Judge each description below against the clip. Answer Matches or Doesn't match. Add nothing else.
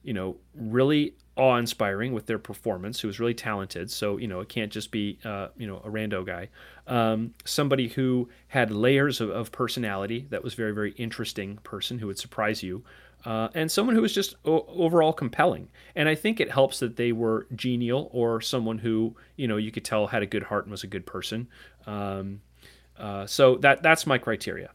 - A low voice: Matches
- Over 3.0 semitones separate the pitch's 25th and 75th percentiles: Matches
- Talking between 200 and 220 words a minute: Matches